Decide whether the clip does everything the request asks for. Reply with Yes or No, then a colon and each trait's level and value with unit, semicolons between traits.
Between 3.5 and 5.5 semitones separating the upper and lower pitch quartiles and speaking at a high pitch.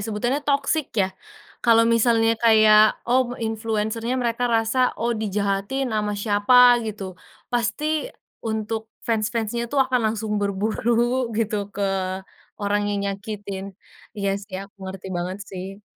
No: average, 2.7 semitones; high, 220 Hz